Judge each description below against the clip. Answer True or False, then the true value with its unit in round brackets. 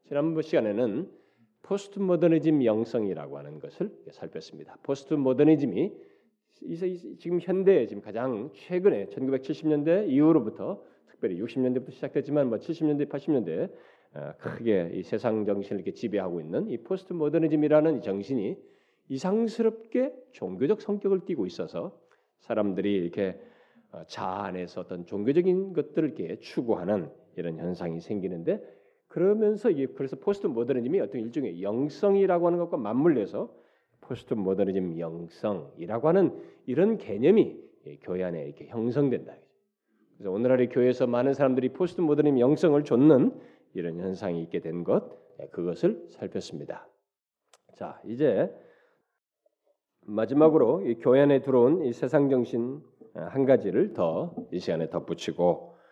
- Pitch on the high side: False (135 Hz)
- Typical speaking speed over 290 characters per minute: True (320 characters per minute)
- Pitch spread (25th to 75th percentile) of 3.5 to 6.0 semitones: False (8.7 semitones)